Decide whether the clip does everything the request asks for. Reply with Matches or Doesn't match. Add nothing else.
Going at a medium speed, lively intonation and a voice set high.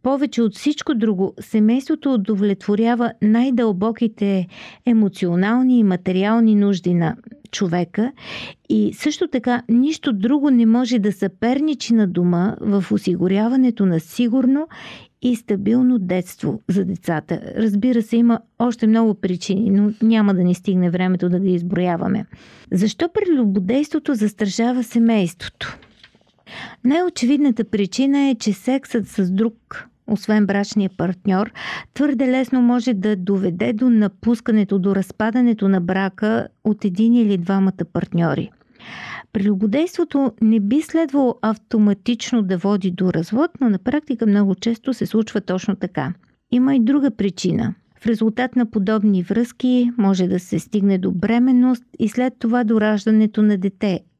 Doesn't match